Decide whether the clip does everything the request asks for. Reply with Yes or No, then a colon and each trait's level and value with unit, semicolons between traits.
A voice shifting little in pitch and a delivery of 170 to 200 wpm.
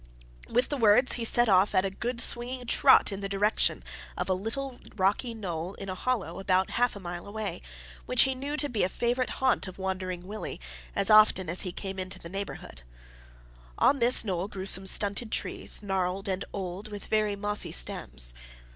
No: average, 3.9 semitones; average, 190 wpm